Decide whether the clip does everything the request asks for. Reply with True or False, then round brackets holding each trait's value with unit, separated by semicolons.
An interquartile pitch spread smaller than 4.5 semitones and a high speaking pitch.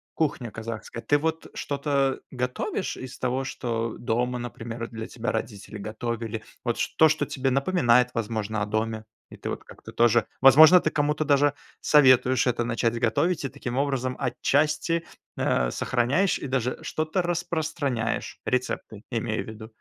False (4.0 semitones; 125 Hz)